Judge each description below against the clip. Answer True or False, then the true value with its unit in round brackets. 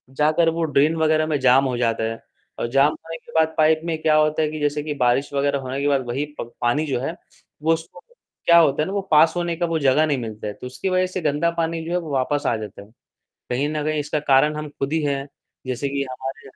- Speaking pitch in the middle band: True (150 Hz)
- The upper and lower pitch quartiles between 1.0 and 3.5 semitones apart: True (2.9 semitones)